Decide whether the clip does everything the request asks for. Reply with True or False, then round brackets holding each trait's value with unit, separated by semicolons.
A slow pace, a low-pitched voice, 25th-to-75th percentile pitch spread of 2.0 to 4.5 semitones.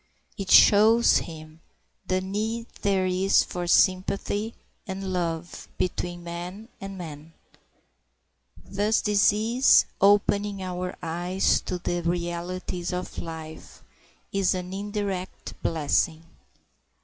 False (100 wpm; 185 Hz; 2.7 semitones)